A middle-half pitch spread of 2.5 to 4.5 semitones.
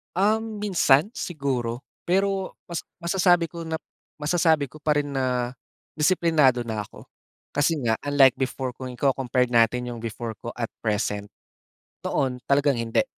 No: wide, 5.6 semitones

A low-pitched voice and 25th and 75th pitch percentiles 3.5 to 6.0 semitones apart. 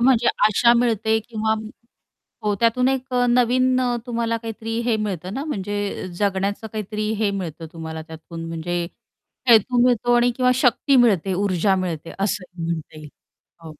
No: high, 215 Hz; average, 4.7 semitones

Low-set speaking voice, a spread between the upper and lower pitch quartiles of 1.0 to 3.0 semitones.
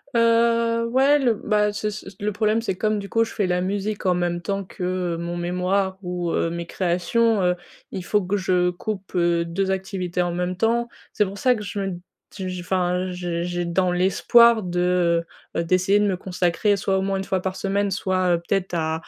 No: high, 190 Hz; average, 2.7 semitones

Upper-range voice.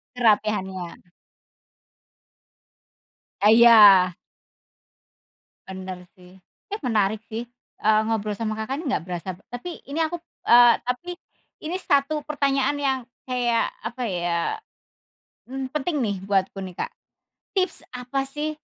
Yes: high, 235 Hz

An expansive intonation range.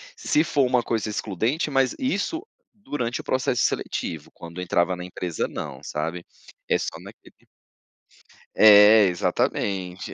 Yes: wide, 6.6 semitones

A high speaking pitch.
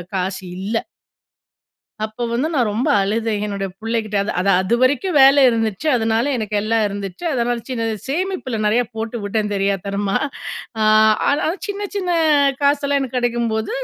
Yes: high, 225 Hz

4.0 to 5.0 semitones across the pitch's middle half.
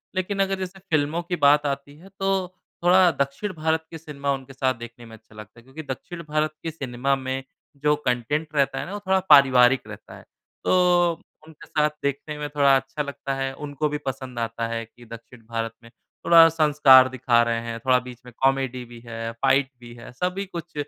Yes: average, 4.5 semitones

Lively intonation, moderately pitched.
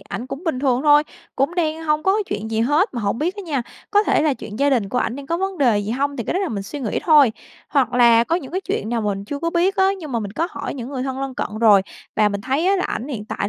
No: wide, 5.9 semitones; very high, 270 Hz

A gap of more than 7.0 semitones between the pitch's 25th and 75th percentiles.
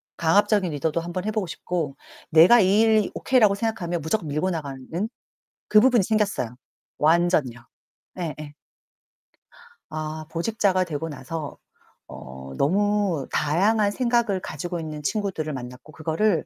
No: average, 5.2 semitones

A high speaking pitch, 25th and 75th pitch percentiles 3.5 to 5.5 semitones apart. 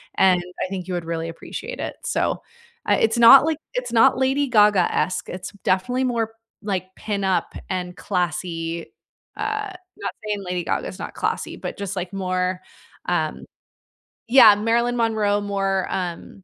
Yes: high, 195 Hz; average, 4.1 semitones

